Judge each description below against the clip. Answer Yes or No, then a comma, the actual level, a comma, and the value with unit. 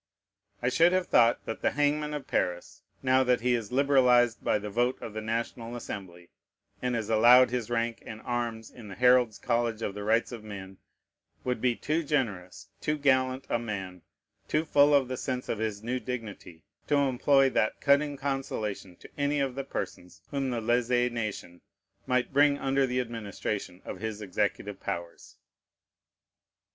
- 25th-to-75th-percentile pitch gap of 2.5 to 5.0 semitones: Yes, average, 3.7 semitones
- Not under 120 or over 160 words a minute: No, average, 175 wpm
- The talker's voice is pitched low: Yes, low, 120 Hz